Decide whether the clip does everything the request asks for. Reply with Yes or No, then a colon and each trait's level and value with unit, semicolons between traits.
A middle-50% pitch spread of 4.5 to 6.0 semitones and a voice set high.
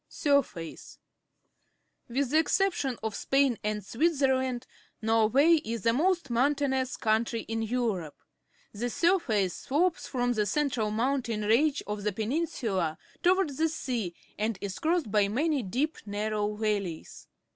Yes: average, 5.0 semitones; high, 240 Hz